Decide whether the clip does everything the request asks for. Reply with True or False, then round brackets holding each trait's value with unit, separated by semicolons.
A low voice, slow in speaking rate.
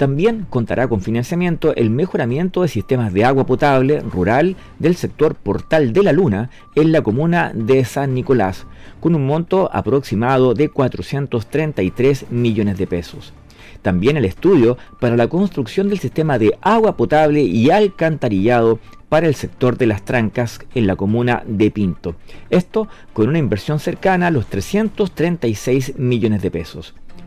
False (130 Hz; 150 wpm)